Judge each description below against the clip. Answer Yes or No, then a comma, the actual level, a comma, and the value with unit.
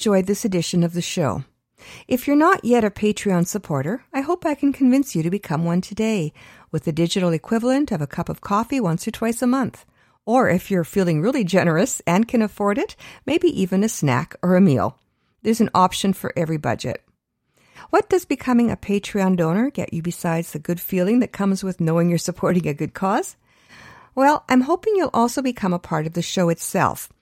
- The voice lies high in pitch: Yes, high, 195 Hz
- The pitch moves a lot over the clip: Yes, wide, 6.4 semitones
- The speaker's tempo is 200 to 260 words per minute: Yes, fast, 205 wpm